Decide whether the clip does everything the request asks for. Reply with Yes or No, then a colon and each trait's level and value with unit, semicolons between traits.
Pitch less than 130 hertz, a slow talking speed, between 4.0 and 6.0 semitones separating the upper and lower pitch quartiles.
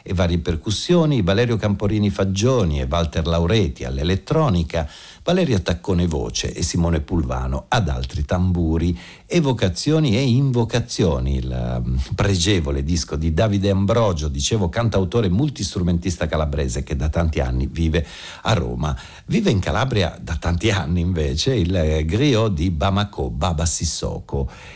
No: very low, 90 Hz; average, 125 wpm; average, 4.4 semitones